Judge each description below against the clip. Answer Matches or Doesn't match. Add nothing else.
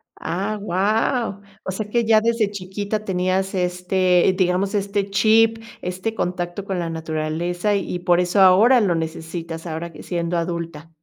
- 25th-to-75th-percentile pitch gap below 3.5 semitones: Matches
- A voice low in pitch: Doesn't match